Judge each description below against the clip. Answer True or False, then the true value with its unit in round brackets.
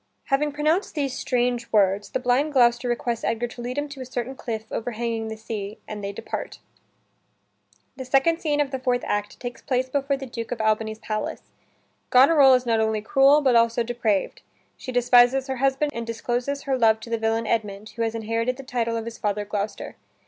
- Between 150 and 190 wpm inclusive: False (200 wpm)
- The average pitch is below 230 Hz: False (240 Hz)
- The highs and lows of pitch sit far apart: False (3.0 semitones)